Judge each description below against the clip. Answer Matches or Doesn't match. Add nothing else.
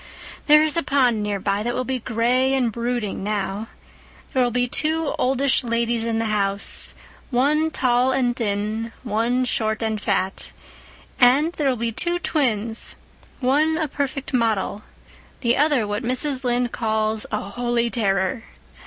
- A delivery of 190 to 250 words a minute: Doesn't match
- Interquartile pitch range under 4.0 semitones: Matches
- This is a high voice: Matches